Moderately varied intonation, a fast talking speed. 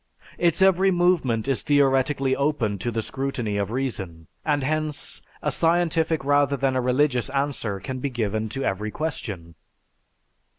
No: average, 5.0 semitones; average, 145 wpm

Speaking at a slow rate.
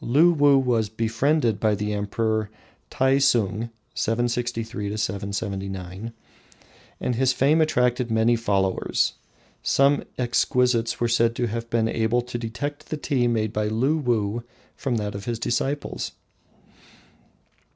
Yes: slow, 120 wpm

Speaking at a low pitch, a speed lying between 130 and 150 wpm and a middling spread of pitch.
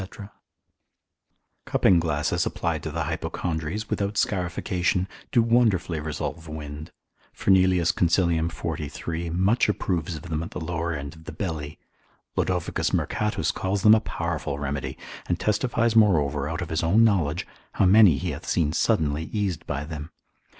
Yes: very low, 85 Hz; average, 145 wpm; average, 3.7 semitones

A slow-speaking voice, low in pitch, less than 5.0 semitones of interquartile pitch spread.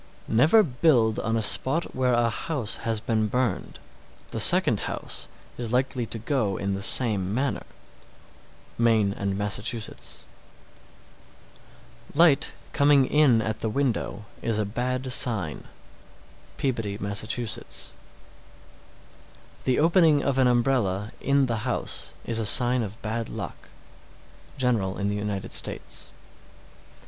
Yes: slow, 130 wpm; low, 115 Hz; average, 3.7 semitones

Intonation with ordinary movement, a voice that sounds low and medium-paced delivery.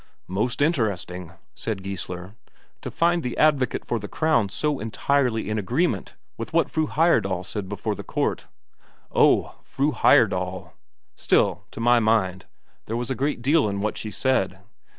No: wide, 6.3 semitones; low, 110 Hz; average, 155 wpm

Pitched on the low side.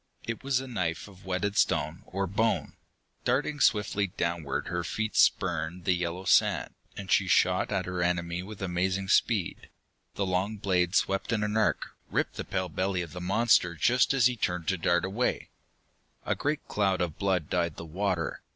Yes: very low, 95 Hz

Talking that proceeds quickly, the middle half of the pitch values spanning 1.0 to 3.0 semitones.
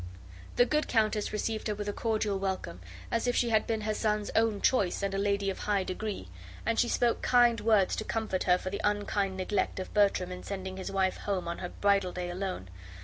Yes: fast, 225 wpm; narrow, 2.6 semitones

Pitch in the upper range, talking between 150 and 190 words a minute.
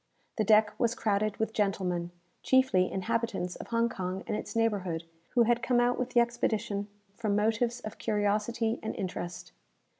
Yes: high, 215 Hz; average, 160 wpm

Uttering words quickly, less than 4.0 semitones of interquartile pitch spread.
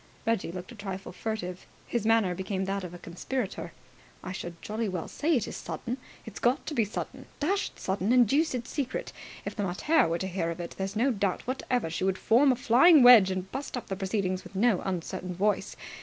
No: fast, 215 wpm; average, 4.7 semitones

